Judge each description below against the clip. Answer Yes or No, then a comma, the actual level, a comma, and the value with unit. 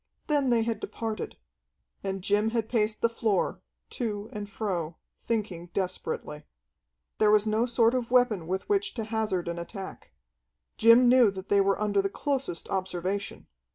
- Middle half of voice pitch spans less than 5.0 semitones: Yes, average, 3.0 semitones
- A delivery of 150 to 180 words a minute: Yes, average, 155 wpm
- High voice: Yes, high, 210 Hz